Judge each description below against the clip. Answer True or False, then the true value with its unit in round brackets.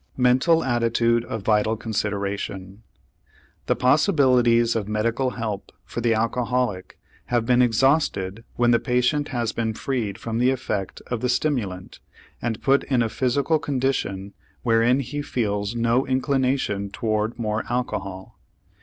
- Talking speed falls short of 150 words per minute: True (135 wpm)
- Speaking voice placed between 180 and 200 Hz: False (120 Hz)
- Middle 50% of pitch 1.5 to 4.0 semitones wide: True (2.9 semitones)